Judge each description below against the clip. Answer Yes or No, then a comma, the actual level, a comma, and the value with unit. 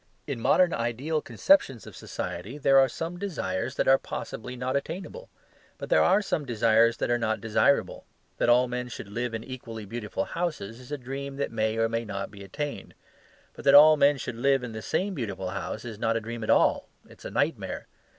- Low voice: Yes, low, 125 Hz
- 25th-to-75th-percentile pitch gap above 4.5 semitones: No, average, 4.0 semitones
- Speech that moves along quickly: Yes, fast, 210 wpm